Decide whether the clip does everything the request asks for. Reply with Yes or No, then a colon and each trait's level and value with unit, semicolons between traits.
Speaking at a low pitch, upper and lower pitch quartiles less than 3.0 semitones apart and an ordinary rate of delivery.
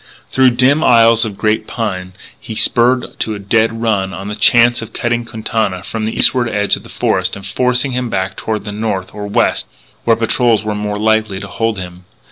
No: low, 110 Hz; narrow, 2.6 semitones; fast, 210 wpm